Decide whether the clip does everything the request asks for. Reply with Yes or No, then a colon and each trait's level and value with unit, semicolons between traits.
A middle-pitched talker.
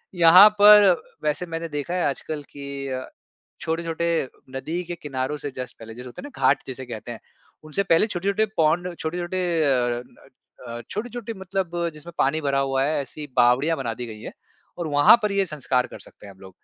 Yes: medium, 155 Hz